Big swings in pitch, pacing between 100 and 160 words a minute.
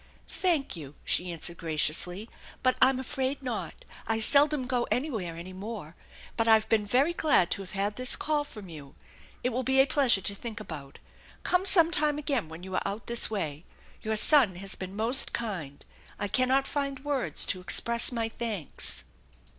No: wide, 6.2 semitones; average, 180 wpm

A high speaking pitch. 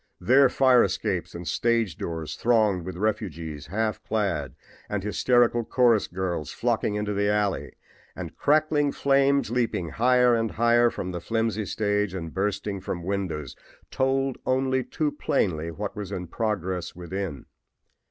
No: low, 105 Hz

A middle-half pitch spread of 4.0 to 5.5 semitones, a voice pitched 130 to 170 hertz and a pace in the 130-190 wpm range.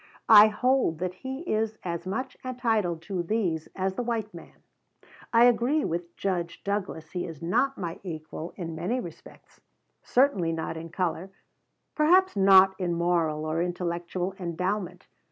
No: average, 4.6 semitones; medium, 185 Hz; average, 150 wpm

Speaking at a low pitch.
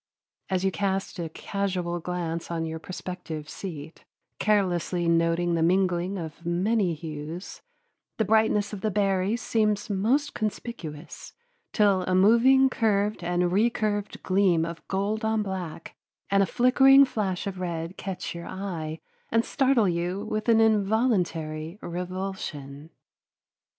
No: high, 190 Hz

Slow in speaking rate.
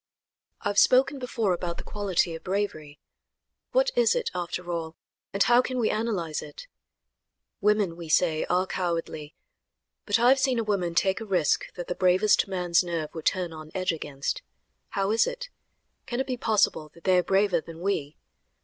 No: average, 185 wpm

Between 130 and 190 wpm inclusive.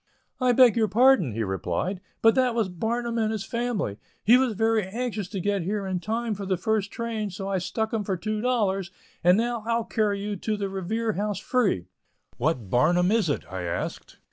No: average, 200 wpm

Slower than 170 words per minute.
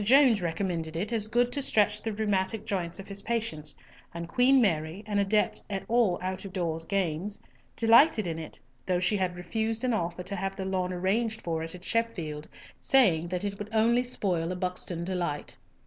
No: average, 195 wpm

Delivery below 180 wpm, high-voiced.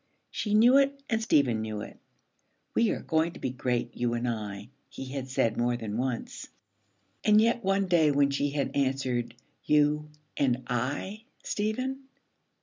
No: average, 160 wpm; medium, 140 Hz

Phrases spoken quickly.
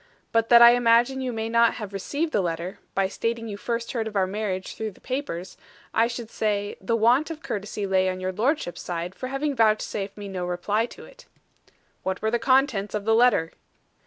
Yes: fast, 210 wpm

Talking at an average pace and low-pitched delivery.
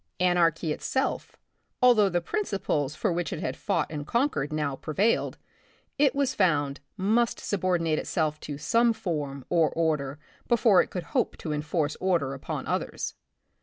No: average, 160 wpm; medium, 170 Hz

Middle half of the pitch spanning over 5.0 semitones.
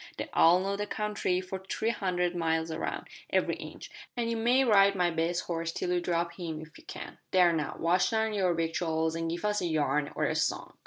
No: average, 3.2 semitones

